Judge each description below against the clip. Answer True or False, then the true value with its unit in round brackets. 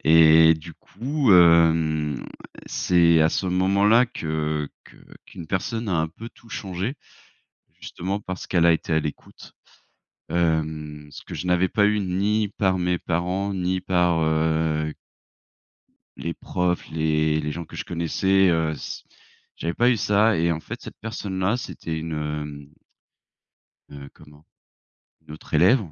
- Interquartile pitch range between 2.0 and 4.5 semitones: True (3.5 semitones)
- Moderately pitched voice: False (85 Hz)